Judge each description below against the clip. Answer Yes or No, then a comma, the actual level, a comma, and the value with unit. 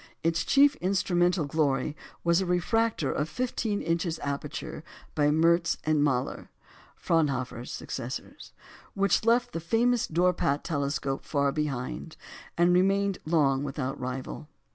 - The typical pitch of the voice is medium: Yes, medium, 160 Hz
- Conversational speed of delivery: No, slow, 125 wpm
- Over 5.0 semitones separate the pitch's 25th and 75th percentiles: No, average, 4.3 semitones